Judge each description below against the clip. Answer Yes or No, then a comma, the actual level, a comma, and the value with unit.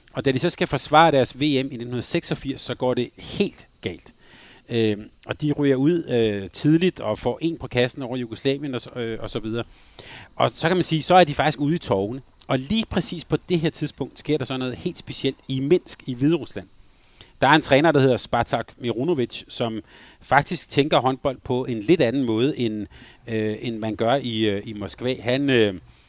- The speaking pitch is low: Yes, low, 130 Hz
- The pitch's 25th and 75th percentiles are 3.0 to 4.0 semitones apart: No, average, 4.4 semitones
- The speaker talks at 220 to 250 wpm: No, average, 205 wpm